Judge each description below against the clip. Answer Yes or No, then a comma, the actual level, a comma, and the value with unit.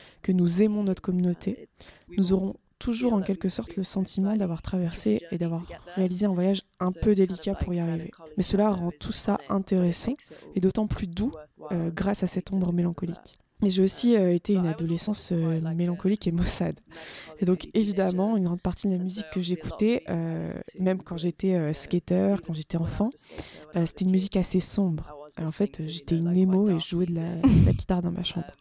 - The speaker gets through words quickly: No, average, 200 wpm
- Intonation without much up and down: Yes, narrow, 2.3 semitones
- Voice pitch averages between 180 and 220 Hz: Yes, medium, 185 Hz